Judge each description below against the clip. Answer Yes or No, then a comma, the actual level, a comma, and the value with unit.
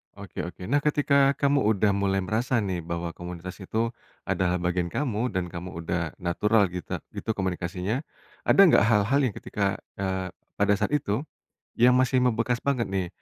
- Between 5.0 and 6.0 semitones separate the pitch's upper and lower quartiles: Yes, average, 5.3 semitones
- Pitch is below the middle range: Yes, low, 100 Hz